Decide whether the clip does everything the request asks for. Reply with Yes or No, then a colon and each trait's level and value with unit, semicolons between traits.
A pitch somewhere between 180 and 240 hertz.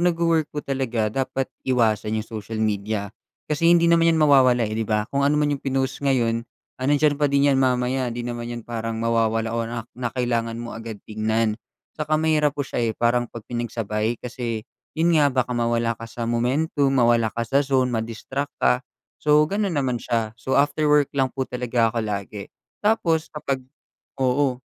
No: low, 125 Hz